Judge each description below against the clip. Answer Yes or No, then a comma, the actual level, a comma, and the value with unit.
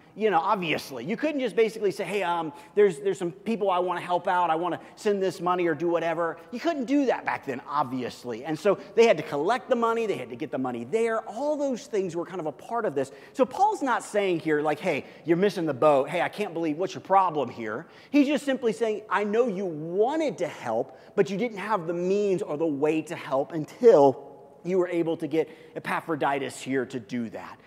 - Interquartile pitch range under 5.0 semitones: No, wide, 5.5 semitones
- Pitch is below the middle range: No, medium, 180 Hz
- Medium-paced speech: No, fast, 240 wpm